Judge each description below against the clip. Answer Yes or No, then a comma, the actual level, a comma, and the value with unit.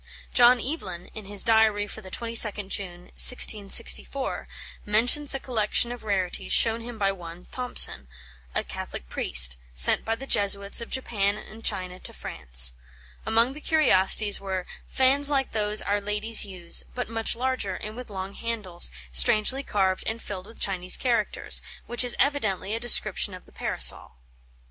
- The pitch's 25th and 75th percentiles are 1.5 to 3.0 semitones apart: No, average, 3.9 semitones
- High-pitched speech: Yes, high, 210 Hz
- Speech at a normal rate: Yes, average, 160 wpm